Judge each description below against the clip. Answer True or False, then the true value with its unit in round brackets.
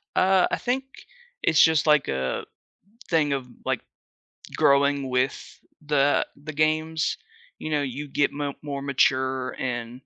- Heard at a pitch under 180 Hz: True (140 Hz)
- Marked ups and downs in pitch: False (2.8 semitones)